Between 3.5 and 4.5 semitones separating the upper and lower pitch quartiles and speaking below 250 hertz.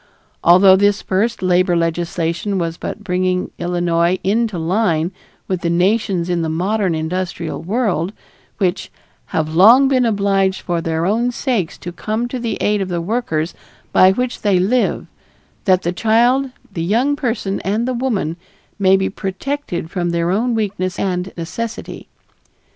Yes: average, 4.1 semitones; high, 190 Hz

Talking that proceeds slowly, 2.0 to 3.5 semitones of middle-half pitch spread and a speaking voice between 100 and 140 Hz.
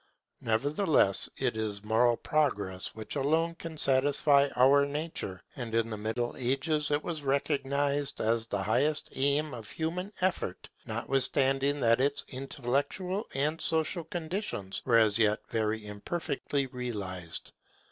No: slow, 130 wpm; average, 5.1 semitones; low, 135 Hz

